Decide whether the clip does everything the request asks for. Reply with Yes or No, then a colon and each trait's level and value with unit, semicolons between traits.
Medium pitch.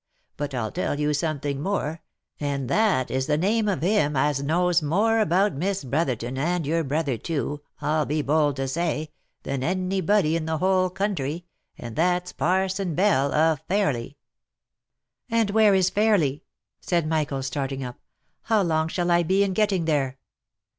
Yes: medium, 160 Hz